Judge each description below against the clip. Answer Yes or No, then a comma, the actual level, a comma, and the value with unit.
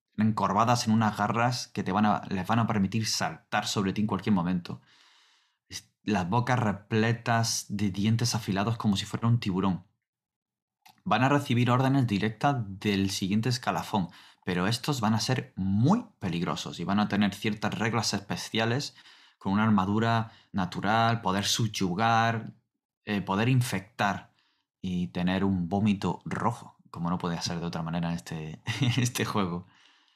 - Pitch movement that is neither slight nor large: Yes, average, 3.0 semitones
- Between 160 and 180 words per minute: No, average, 150 wpm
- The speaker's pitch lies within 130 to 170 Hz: No, low, 105 Hz